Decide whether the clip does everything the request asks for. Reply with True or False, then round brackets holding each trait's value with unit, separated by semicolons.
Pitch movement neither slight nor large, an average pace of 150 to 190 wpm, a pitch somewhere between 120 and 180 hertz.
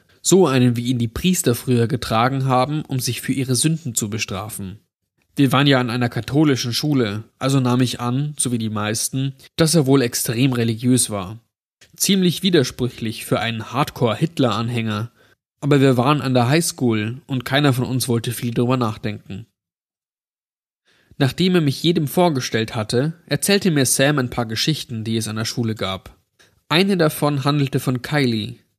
True (3.8 semitones; 165 wpm; 125 Hz)